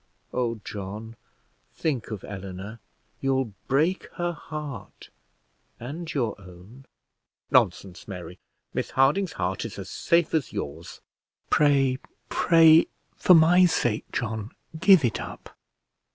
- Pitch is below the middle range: Yes, low, 130 Hz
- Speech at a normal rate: No, slow, 115 wpm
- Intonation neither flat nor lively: No, wide, 7.4 semitones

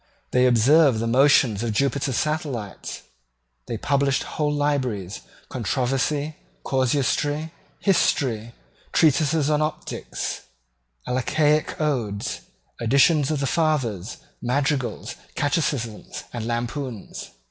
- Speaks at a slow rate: Yes, slow, 95 wpm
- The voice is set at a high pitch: No, low, 135 Hz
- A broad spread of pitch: No, average, 4.0 semitones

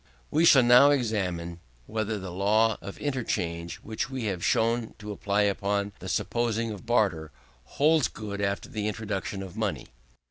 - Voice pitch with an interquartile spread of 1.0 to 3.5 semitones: Yes, average, 2.9 semitones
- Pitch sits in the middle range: No, low, 105 Hz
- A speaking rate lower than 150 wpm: No, average, 170 wpm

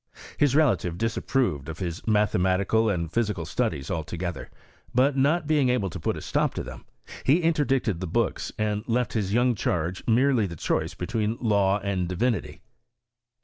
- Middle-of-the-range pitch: No, low, 105 Hz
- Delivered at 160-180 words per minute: Yes, average, 170 wpm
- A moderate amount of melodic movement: No, wide, 5.7 semitones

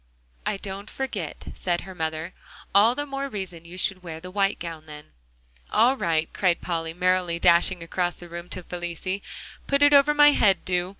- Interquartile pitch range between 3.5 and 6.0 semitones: No, average, 3.1 semitones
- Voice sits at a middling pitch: Yes, medium, 180 Hz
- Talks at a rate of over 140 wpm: Yes, average, 185 wpm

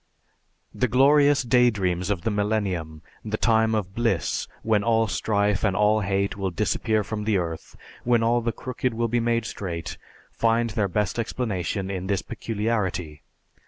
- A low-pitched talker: Yes, low, 105 Hz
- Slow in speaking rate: No, average, 160 wpm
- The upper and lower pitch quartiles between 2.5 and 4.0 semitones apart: Yes, average, 3.2 semitones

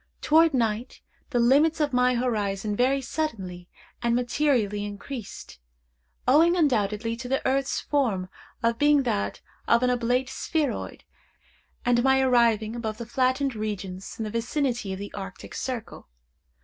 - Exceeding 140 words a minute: No, slow, 135 wpm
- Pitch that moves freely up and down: No, average, 4.1 semitones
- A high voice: Yes, high, 240 Hz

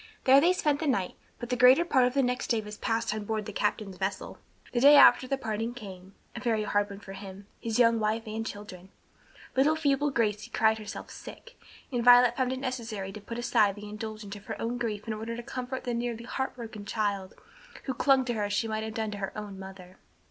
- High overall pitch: Yes, high, 225 Hz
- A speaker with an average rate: No, fast, 235 wpm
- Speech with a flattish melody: No, average, 3.2 semitones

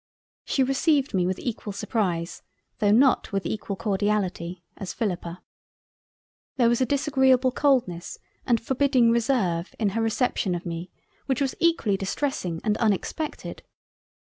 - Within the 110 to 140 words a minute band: Yes, slow, 135 wpm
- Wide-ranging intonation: Yes, wide, 5.9 semitones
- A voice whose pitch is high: Yes, high, 220 Hz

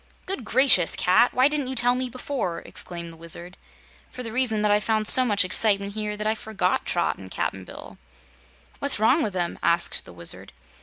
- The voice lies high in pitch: Yes, high, 215 Hz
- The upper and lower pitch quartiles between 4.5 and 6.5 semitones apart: Yes, wide, 5.5 semitones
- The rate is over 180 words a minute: Yes, average, 200 wpm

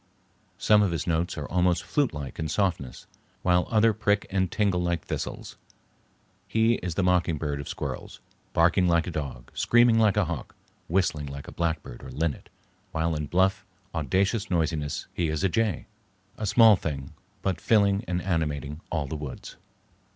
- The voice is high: No, very low, 85 Hz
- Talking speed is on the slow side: No, average, 165 wpm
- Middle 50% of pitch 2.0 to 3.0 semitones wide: No, average, 4.2 semitones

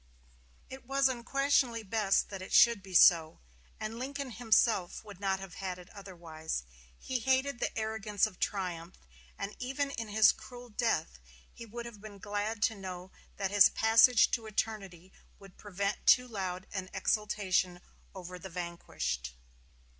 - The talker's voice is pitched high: Yes, high, 205 Hz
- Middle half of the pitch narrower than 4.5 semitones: Yes, average, 3.7 semitones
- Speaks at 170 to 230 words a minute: No, average, 155 wpm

